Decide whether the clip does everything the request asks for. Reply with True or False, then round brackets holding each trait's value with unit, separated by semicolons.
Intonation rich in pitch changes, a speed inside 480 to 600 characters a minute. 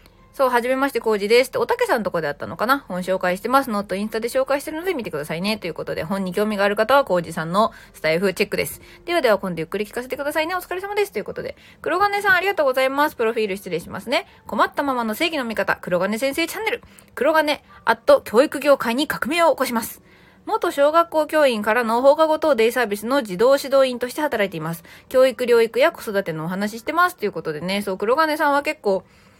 True (7.3 semitones; 500 characters per minute)